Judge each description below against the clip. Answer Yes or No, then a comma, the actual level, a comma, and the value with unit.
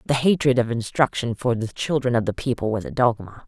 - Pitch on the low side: Yes, low, 125 Hz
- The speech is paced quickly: Yes, fast, 225 wpm